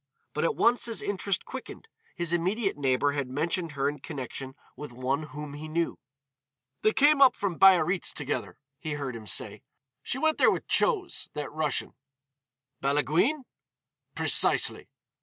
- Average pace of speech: Yes, average, 150 wpm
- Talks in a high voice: No, medium, 155 Hz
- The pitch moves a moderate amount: No, wide, 6.1 semitones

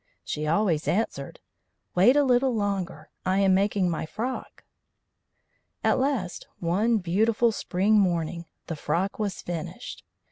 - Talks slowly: Yes, slow, 130 wpm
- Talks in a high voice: Yes, high, 195 Hz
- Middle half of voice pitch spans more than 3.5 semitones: Yes, average, 4.2 semitones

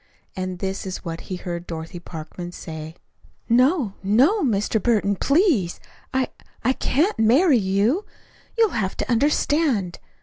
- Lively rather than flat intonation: Yes, wide, 7.0 semitones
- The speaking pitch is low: No, high, 210 Hz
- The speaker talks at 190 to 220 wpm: No, slow, 135 wpm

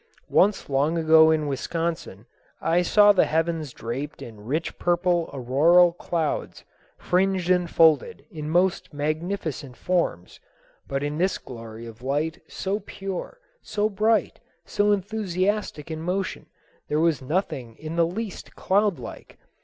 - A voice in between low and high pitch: Yes, medium, 165 Hz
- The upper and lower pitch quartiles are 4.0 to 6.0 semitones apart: Yes, average, 4.3 semitones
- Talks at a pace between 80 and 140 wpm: Yes, slow, 135 wpm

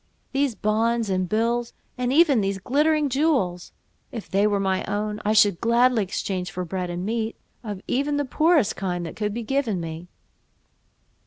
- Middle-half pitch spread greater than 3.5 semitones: Yes, average, 4.7 semitones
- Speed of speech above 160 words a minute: Yes, average, 170 wpm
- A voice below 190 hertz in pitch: No, high, 215 Hz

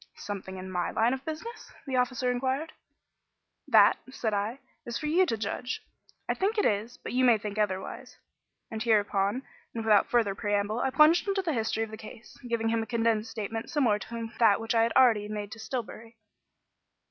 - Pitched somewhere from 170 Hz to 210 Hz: No, high, 225 Hz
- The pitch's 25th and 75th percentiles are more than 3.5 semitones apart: No, average, 3.2 semitones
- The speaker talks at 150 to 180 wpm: No, average, 190 wpm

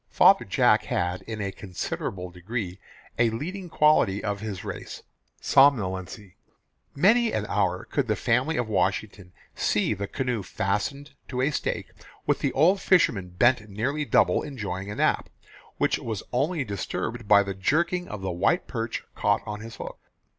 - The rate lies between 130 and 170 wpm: Yes, average, 160 wpm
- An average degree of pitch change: No, wide, 6.0 semitones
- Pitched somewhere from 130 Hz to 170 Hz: No, low, 110 Hz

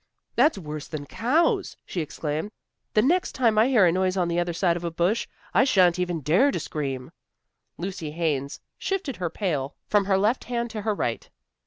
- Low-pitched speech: No, medium, 185 Hz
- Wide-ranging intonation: Yes, wide, 5.7 semitones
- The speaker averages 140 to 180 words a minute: No, average, 195 wpm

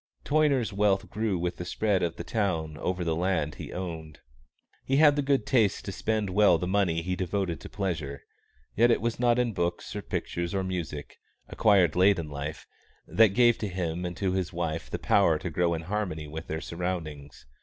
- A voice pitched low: Yes, very low, 90 Hz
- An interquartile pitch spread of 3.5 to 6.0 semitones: Yes, average, 3.8 semitones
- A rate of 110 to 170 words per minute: No, average, 200 wpm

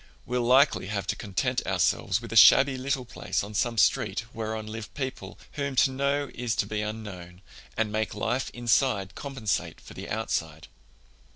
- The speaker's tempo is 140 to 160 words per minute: No, average, 170 wpm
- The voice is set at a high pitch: No, low, 115 Hz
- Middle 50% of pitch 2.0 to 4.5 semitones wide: Yes, average, 3.9 semitones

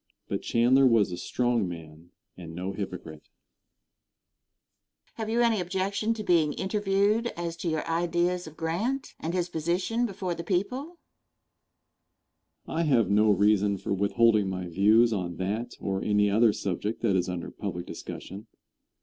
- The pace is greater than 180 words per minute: No, average, 155 wpm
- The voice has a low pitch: Yes, low, 120 Hz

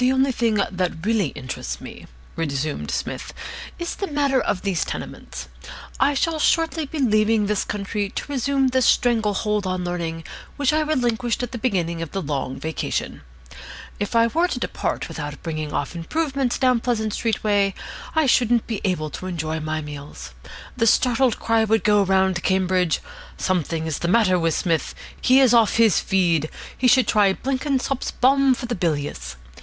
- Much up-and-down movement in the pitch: Yes, wide, 6.7 semitones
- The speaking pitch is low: No, high, 210 Hz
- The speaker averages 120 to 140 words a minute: No, average, 175 wpm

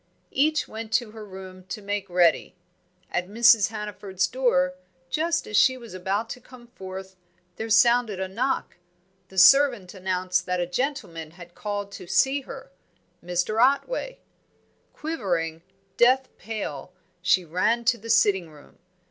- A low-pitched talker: No, high, 205 Hz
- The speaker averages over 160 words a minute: No, average, 145 wpm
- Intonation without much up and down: No, average, 4.8 semitones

